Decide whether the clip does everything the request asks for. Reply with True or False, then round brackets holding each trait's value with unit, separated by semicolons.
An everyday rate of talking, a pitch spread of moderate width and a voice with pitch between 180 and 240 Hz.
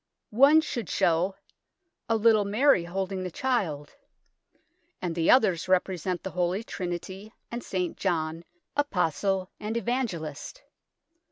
False (120 wpm; 4.6 semitones; 190 Hz)